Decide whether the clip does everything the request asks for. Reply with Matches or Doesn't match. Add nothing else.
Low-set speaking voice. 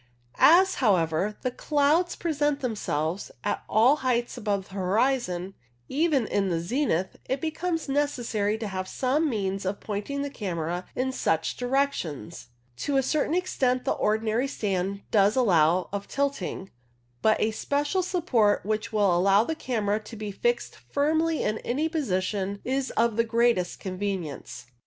Doesn't match